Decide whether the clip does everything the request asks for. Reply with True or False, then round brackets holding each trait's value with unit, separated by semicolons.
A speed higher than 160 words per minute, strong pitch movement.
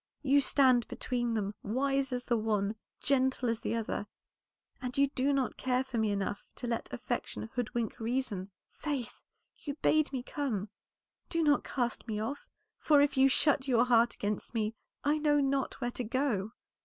False (175 wpm; 3.6 semitones)